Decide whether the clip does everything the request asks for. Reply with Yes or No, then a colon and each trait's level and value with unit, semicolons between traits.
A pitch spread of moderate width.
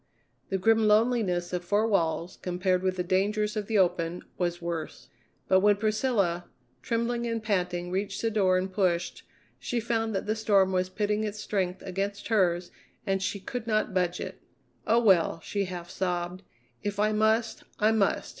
Yes: average, 3.1 semitones